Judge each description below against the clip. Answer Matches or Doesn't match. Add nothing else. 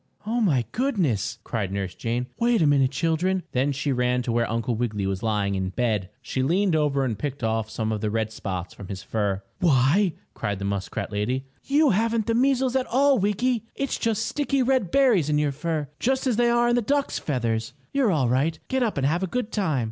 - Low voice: Doesn't match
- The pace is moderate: Doesn't match